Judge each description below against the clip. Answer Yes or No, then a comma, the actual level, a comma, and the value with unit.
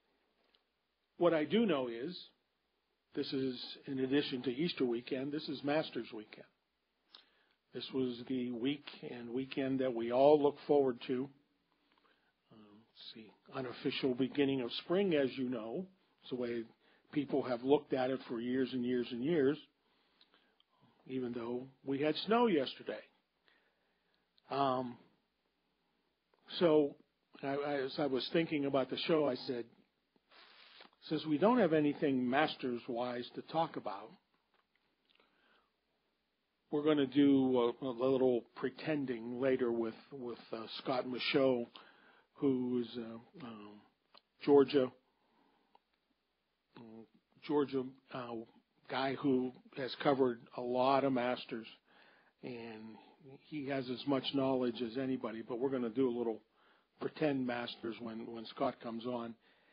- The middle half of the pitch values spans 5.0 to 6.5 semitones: No, average, 2.7 semitones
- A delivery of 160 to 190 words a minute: No, slow, 135 wpm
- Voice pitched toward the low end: Yes, low, 130 Hz